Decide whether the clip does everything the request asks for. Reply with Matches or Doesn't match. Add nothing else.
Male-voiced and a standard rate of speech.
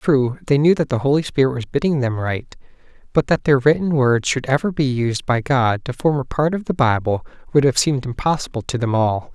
Doesn't match